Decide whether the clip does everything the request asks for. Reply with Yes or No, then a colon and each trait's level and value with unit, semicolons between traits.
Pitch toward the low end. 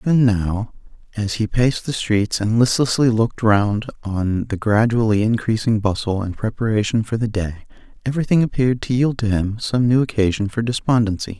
Yes: low, 110 Hz